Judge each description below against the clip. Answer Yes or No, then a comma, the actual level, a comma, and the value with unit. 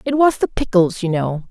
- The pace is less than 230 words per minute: No, fast, 240 wpm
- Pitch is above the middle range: Yes, high, 200 Hz